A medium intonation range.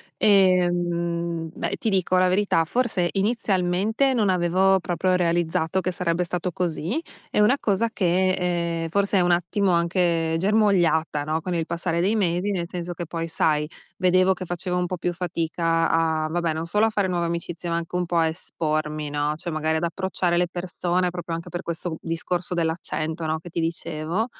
No: narrow, 2.0 semitones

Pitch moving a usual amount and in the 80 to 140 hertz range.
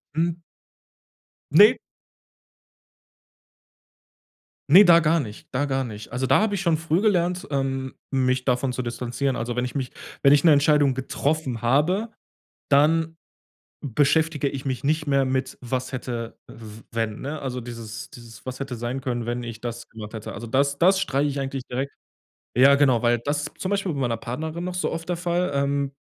Yes: average, 4.1 semitones; low, 135 Hz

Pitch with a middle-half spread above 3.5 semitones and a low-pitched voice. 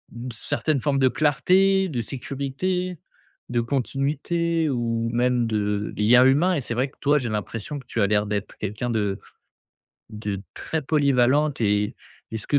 Yes: average, 4.7 semitones; low, 125 Hz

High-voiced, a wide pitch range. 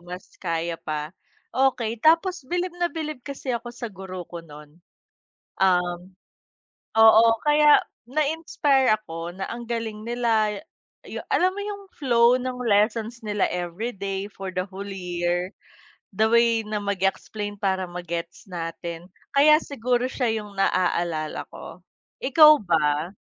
Yes: high, 210 Hz; wide, 5.8 semitones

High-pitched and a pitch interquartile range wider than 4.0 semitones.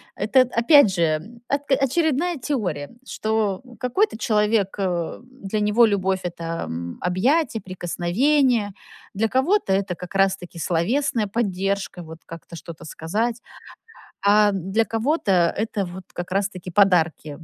Yes: high, 200 Hz; average, 5.0 semitones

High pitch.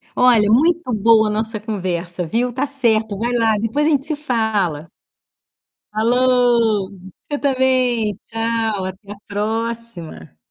Yes: high, 225 Hz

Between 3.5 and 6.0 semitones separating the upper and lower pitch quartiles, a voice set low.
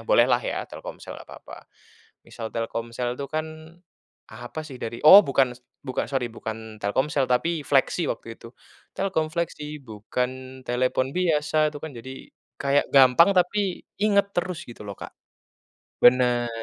Yes: average, 4.5 semitones; low, 130 Hz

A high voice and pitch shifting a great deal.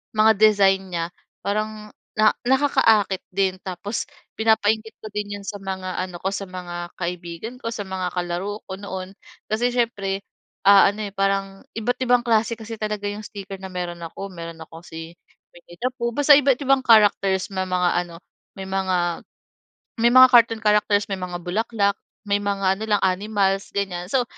No: high, 200 Hz; average, 2.9 semitones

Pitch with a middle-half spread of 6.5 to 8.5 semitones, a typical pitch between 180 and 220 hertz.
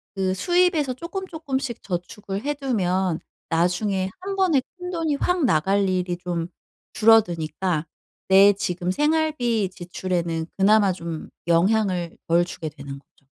Yes: wide, 7.4 semitones; high, 195 Hz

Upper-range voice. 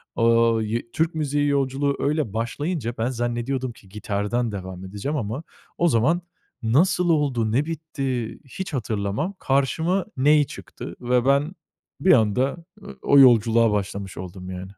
No: low, 125 Hz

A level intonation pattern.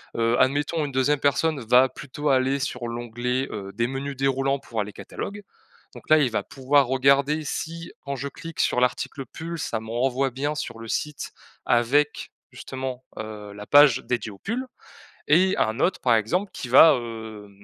No: average, 3.6 semitones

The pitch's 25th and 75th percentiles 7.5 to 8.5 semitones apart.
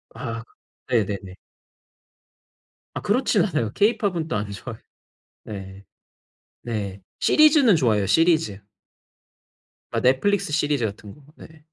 Yes: wide, 8.2 semitones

